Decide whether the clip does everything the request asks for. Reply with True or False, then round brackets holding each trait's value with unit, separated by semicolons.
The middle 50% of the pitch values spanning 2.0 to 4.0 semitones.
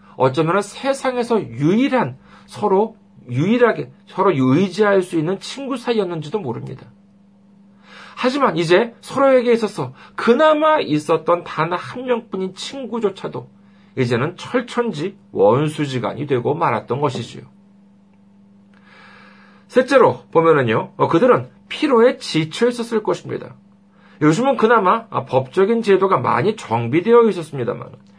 False (5.4 semitones)